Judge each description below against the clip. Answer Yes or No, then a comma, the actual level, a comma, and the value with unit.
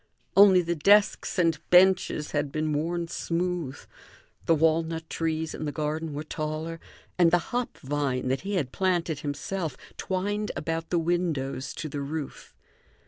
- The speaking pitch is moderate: Yes, medium, 165 Hz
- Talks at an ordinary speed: Yes, average, 150 wpm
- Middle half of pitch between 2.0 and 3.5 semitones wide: Yes, average, 2.9 semitones